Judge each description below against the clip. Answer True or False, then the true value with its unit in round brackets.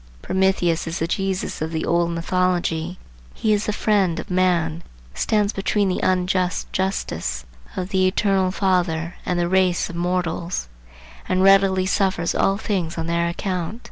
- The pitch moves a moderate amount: False (2.1 semitones)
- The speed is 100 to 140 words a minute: False (155 wpm)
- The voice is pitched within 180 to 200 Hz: True (185 Hz)